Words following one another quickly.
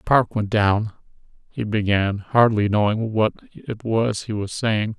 No: average, 155 wpm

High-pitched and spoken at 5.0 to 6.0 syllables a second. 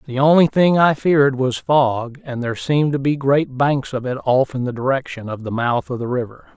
No: low, 135 Hz; 5.3 syllables/s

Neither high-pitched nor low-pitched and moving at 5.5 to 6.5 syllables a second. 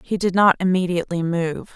Yes: medium, 180 Hz; 5.6 syllables/s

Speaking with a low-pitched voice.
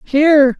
No: very high, 255 Hz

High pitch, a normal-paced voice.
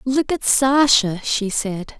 Yes: high, 240 Hz; average, 150 wpm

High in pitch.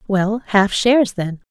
Yes: high, 205 Hz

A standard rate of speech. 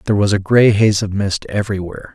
No: fast, 225 wpm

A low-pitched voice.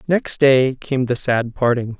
Yes: low, 130 Hz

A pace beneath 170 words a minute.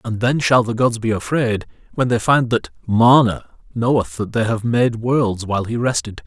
No: average, 200 wpm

